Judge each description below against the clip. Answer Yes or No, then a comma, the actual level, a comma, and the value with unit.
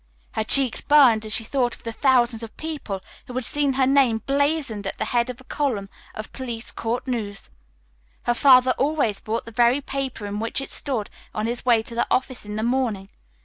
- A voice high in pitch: Yes, high, 240 Hz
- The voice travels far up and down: No, average, 3.3 semitones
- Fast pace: Yes, fast, 210 wpm